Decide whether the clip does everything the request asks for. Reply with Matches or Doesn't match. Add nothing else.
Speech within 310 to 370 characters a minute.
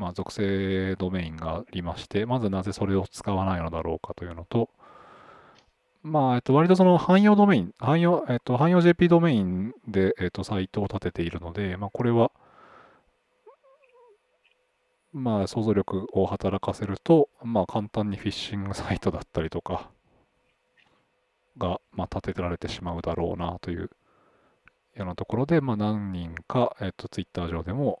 Doesn't match